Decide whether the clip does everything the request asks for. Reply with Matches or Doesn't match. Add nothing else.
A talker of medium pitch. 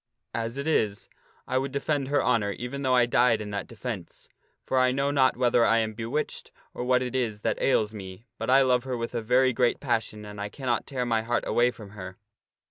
Doesn't match